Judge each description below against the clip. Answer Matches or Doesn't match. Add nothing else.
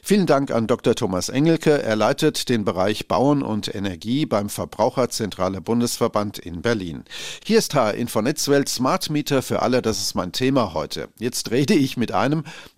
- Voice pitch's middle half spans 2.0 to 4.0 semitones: Doesn't match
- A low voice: Matches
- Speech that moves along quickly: Doesn't match